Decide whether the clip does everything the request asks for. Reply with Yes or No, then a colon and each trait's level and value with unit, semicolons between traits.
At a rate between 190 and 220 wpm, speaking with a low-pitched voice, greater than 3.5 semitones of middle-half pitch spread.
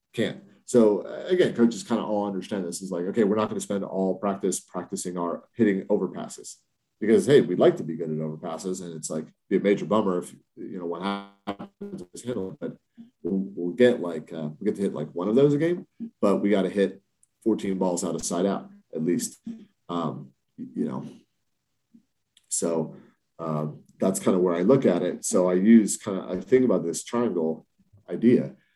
Yes: average, 200 wpm; very low, 95 Hz; average, 5.2 semitones